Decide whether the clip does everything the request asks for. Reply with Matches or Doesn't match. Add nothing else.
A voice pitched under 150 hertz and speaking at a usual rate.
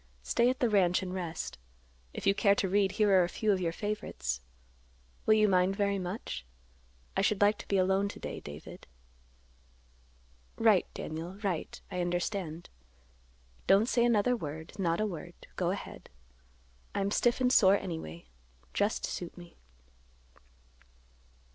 Doesn't match